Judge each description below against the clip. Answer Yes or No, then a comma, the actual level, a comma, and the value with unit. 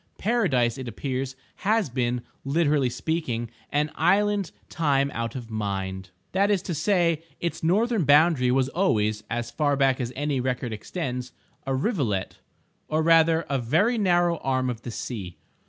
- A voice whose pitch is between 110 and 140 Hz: Yes, low, 135 Hz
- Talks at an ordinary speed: Yes, average, 150 wpm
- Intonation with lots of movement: Yes, wide, 5.9 semitones